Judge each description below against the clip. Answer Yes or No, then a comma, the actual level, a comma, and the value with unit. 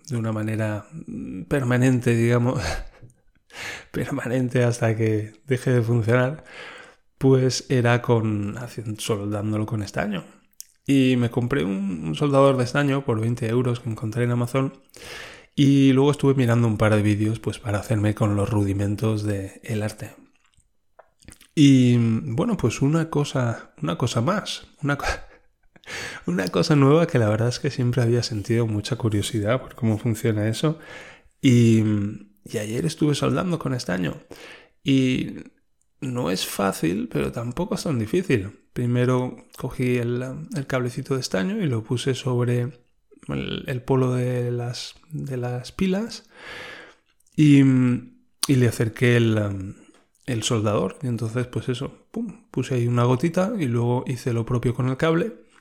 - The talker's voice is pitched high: No, low, 125 Hz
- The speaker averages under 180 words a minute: Yes, average, 145 wpm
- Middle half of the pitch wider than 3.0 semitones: Yes, average, 3.4 semitones